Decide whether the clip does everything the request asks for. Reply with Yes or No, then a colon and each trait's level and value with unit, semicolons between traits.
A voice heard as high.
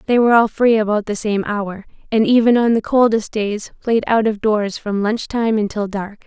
Yes: high, 215 Hz